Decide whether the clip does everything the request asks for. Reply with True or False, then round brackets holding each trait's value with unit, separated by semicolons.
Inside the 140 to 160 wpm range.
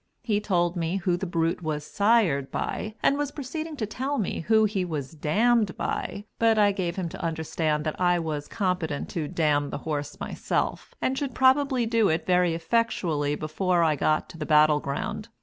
False (190 wpm)